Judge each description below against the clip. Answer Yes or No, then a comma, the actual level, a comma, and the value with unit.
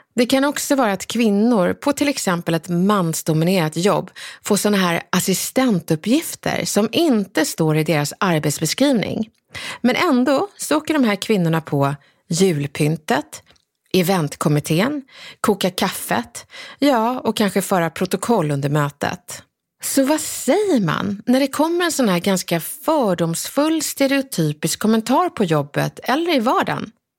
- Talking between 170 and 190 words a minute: No, average, 130 wpm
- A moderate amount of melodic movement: No, wide, 8.2 semitones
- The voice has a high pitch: Yes, high, 200 Hz